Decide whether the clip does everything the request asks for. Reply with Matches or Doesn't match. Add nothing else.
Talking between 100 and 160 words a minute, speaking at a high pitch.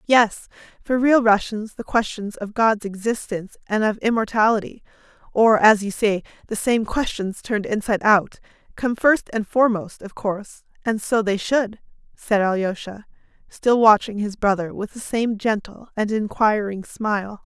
Matches